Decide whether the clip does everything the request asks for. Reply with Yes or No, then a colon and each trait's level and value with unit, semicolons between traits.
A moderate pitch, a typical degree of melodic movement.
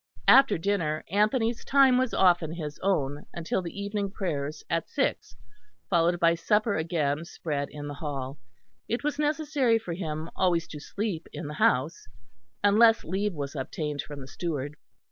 No: medium, 170 Hz; wide, 5.7 semitones